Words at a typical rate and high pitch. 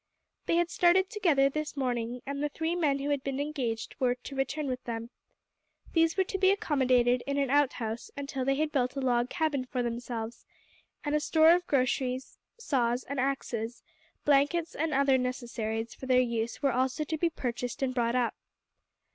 Yes: average, 185 wpm; very high, 270 Hz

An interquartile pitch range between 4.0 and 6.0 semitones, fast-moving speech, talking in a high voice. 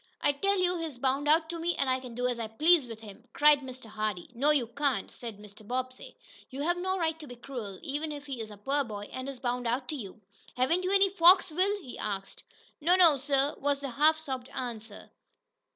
Yes: average, 4.9 semitones; fast, 230 wpm; very high, 270 Hz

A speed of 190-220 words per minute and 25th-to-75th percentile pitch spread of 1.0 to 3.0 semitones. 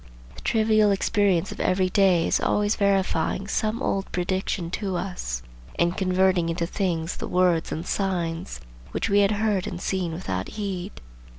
No: average, 160 wpm; narrow, 2.6 semitones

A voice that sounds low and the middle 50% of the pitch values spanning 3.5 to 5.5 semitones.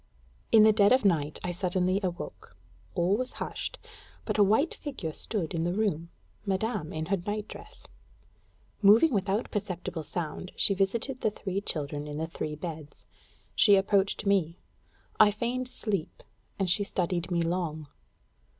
No: high, 190 Hz; average, 3.8 semitones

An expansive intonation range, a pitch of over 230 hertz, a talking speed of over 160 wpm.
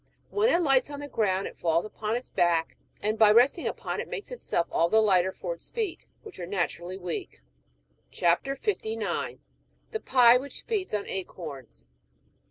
No: wide, 8.4 semitones; high, 220 Hz; average, 175 wpm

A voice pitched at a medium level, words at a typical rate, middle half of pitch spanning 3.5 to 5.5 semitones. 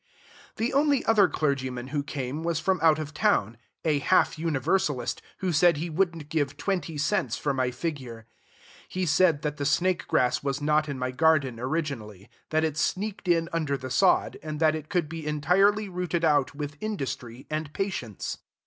Yes: medium, 155 Hz; average, 175 wpm; average, 3.8 semitones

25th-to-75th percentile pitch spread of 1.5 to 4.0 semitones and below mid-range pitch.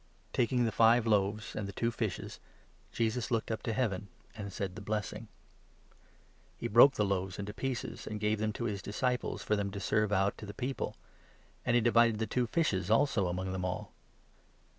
Yes: average, 2.7 semitones; low, 110 Hz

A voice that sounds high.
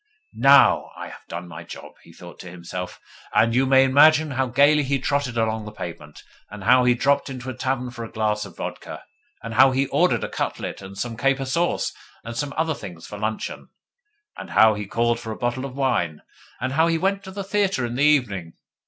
No: low, 125 Hz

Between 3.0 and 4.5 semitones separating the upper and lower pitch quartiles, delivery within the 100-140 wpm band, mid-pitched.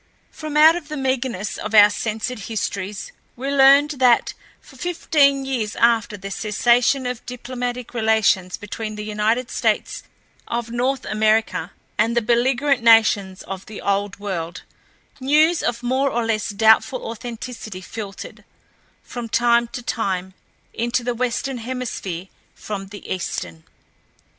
No: average, 3.3 semitones; slow, 135 wpm; high, 235 Hz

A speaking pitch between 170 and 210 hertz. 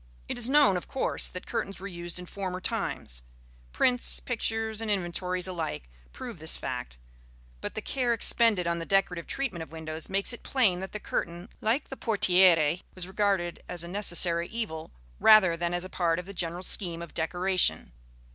Yes: medium, 185 Hz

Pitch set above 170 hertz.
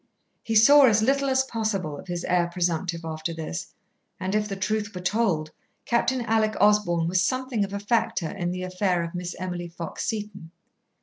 Yes: high, 190 Hz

